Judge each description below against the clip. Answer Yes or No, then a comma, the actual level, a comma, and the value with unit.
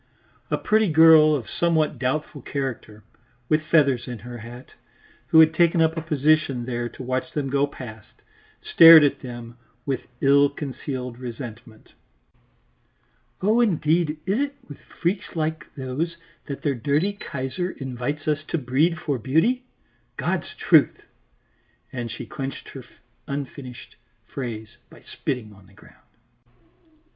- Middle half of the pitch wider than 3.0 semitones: Yes, average, 4.2 semitones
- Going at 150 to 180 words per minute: No, slow, 135 wpm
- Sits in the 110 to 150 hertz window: Yes, medium, 140 Hz